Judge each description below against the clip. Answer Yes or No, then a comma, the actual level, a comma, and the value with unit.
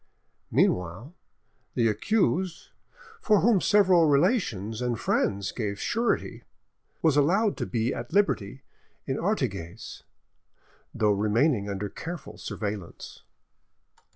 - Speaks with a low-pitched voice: Yes, low, 125 Hz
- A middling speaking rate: No, slow, 100 wpm